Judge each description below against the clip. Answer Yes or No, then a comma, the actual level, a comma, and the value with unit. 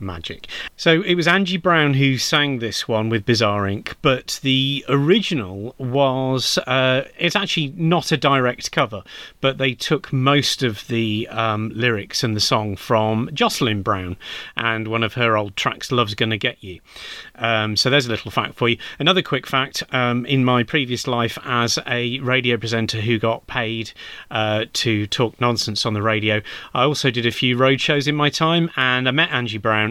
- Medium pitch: No, low, 125 Hz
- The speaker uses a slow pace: No, average, 185 wpm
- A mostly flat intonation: No, average, 3.8 semitones